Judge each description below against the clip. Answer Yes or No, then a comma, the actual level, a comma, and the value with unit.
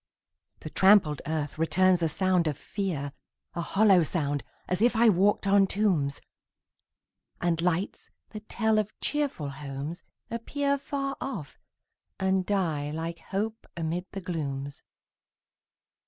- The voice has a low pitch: No, medium, 180 Hz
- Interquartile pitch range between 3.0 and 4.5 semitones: No, average, 5.0 semitones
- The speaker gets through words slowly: Yes, slow, 125 wpm